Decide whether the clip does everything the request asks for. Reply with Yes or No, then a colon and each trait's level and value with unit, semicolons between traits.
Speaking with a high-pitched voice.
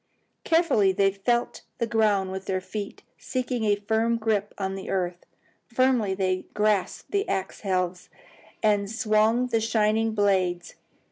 Yes: high, 210 Hz